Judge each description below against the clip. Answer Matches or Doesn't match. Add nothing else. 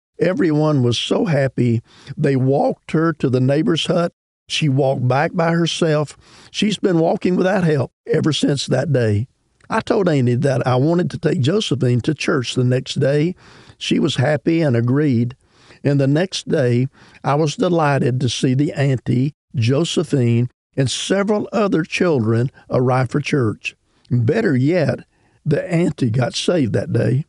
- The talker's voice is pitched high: Doesn't match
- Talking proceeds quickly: Doesn't match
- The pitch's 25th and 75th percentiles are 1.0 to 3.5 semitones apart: Doesn't match